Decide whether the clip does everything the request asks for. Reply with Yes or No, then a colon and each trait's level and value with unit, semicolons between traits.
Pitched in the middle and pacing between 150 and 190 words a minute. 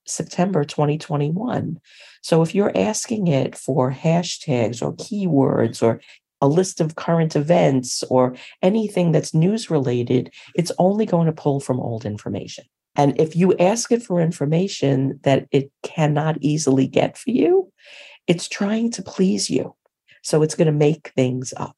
Yes: medium, 160 Hz; average, 155 wpm